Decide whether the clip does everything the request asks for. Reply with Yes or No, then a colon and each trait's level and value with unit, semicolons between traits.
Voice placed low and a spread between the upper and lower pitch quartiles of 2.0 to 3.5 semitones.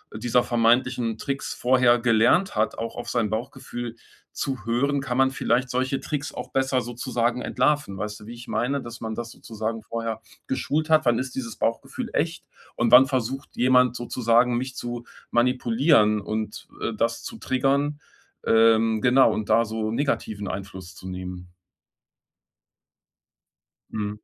Yes: low, 120 Hz; narrow, 2.6 semitones